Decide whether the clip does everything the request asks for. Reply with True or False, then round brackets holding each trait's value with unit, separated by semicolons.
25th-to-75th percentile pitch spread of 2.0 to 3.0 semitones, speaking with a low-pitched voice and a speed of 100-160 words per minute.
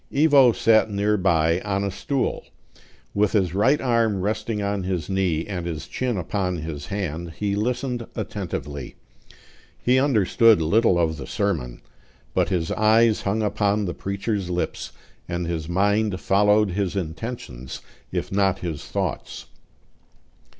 False (3.8 semitones; 100 Hz; 140 wpm)